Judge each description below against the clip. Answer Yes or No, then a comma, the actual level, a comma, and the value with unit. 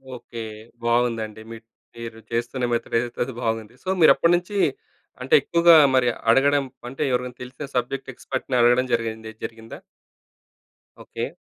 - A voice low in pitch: Yes, low, 120 Hz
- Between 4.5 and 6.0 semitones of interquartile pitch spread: No, average, 2.7 semitones